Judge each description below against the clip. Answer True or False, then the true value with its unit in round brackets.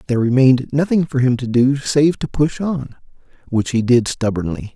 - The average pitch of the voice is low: True (130 Hz)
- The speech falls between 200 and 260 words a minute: False (190 wpm)